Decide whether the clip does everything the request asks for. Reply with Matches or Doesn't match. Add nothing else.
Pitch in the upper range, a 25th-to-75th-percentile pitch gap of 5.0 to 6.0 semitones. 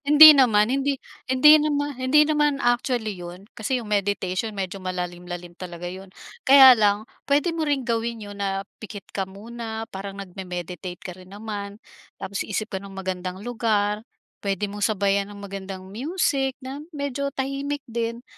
Matches